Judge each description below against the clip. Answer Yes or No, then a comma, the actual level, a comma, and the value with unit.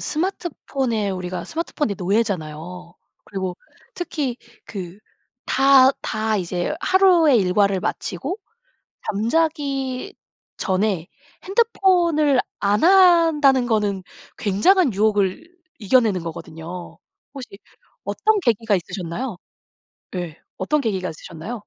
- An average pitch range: No, wide, 8.3 semitones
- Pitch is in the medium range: No, high, 220 Hz